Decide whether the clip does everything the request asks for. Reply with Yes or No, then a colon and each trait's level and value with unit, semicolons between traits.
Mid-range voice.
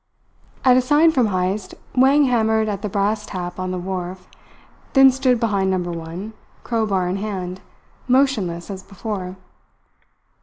No: high, 200 Hz